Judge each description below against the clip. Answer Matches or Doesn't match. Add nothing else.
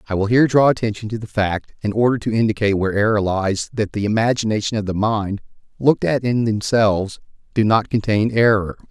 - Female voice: Doesn't match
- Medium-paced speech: Matches